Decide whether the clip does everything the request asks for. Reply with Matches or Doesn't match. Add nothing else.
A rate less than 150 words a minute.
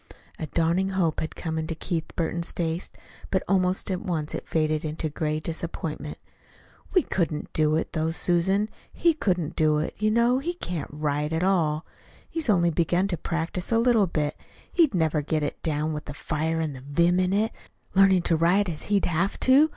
Doesn't match